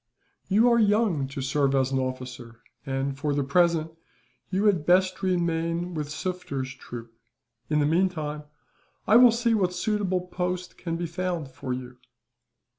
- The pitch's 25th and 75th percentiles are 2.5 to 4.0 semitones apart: No, average, 5.2 semitones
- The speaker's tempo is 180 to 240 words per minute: No, average, 155 wpm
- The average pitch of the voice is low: No, medium, 165 Hz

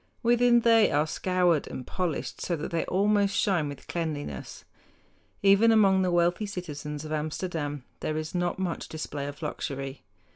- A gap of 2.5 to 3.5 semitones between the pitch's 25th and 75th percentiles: No, average, 4.6 semitones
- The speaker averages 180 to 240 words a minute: No, average, 155 wpm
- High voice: No, medium, 170 Hz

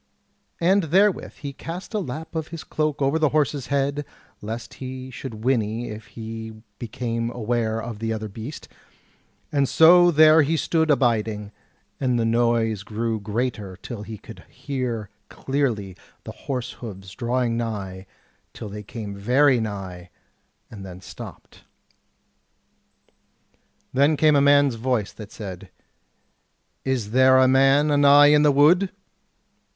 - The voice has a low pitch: Yes, low, 120 Hz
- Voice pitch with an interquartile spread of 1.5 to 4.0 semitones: No, average, 4.7 semitones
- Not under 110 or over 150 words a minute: Yes, average, 140 wpm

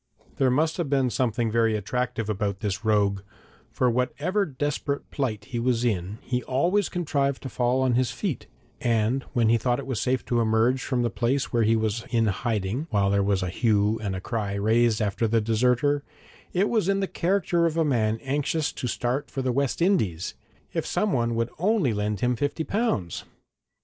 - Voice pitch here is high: No, low, 120 Hz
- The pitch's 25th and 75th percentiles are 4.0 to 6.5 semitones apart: Yes, average, 4.4 semitones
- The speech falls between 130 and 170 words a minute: No, average, 190 wpm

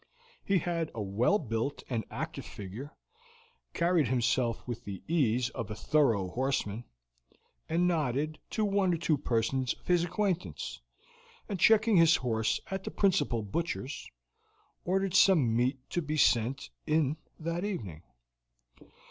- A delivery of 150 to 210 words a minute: No, average, 140 wpm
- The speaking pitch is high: No, medium, 145 Hz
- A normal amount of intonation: No, wide, 6.9 semitones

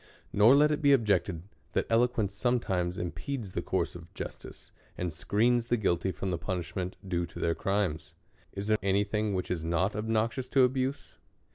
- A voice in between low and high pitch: No, low, 100 Hz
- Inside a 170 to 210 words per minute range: Yes, average, 180 wpm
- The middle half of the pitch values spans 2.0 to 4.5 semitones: No, average, 5.1 semitones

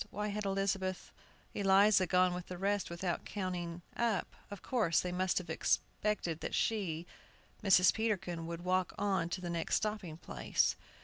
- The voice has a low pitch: No, medium, 185 Hz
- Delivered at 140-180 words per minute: Yes, average, 160 wpm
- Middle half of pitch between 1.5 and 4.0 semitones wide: Yes, narrow, 2.6 semitones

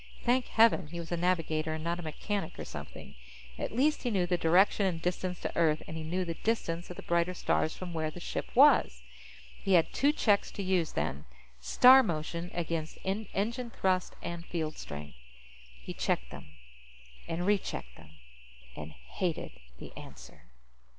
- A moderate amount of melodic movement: Yes, average, 3.5 semitones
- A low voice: No, medium, 175 Hz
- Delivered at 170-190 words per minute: Yes, average, 175 wpm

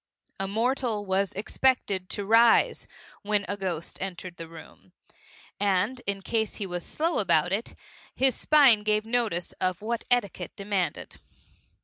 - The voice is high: Yes, high, 205 Hz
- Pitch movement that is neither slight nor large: Yes, average, 3.7 semitones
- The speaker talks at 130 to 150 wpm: Yes, average, 140 wpm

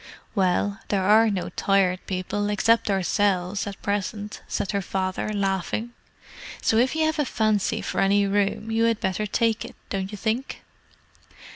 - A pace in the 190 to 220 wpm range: No, average, 160 wpm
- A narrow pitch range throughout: Yes, narrow, 2.2 semitones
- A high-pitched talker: Yes, high, 205 Hz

